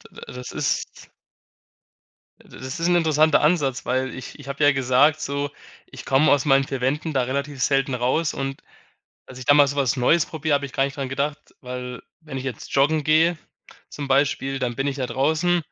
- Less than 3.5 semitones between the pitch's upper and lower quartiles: Yes, narrow, 2.4 semitones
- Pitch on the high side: No, medium, 140 Hz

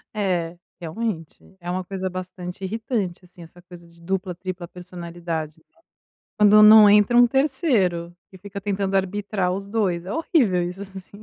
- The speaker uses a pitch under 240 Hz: Yes, medium, 185 Hz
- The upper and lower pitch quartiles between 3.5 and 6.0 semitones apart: No, average, 2.8 semitones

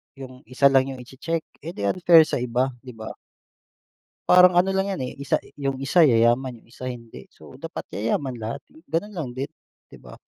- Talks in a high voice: No, low, 135 Hz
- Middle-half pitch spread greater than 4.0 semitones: Yes, average, 5.1 semitones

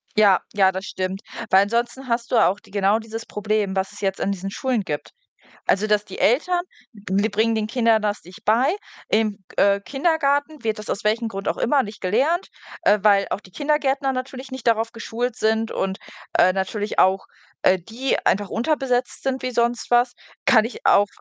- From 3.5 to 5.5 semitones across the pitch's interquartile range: Yes, average, 4.0 semitones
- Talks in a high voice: Yes, high, 220 Hz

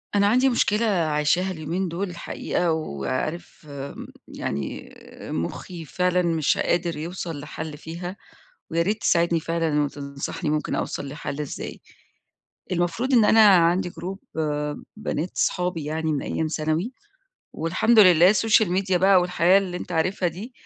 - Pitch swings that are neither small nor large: Yes, average, 3.2 semitones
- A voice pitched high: No, medium, 170 Hz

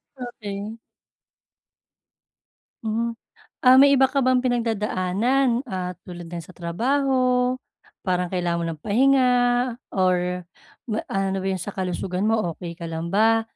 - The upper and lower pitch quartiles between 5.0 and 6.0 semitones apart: Yes, wide, 5.5 semitones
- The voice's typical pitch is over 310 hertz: No, high, 205 Hz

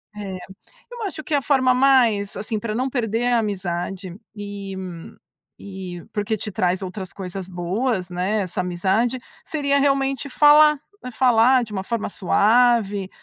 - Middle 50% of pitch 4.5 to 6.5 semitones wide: Yes, average, 5.1 semitones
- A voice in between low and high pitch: No, high, 215 Hz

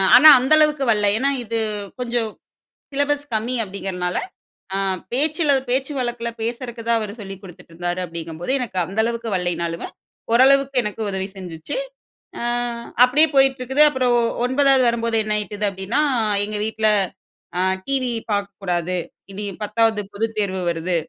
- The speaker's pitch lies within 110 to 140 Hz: No, high, 225 Hz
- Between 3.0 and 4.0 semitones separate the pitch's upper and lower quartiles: No, average, 5.0 semitones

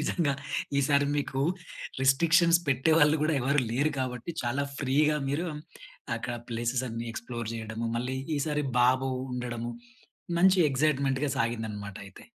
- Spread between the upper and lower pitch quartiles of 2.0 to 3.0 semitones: No, average, 3.8 semitones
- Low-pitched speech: Yes, low, 130 Hz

